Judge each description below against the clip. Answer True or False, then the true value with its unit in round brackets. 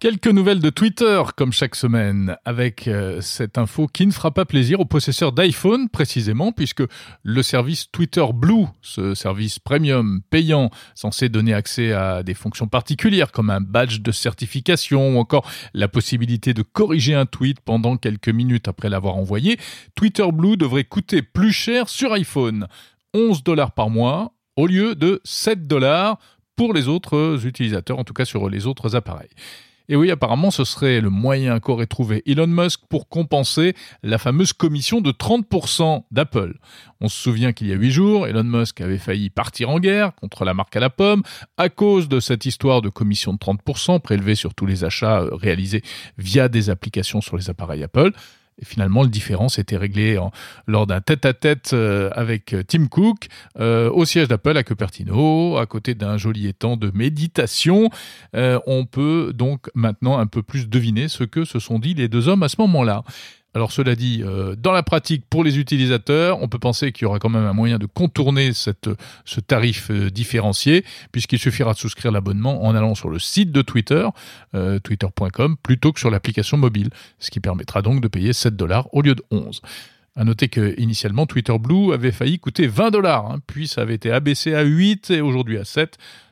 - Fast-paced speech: False (185 wpm)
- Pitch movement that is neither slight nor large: False (6.1 semitones)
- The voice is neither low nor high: False (125 Hz)